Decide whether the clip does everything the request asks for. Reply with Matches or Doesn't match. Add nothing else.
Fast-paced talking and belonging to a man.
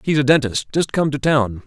Matches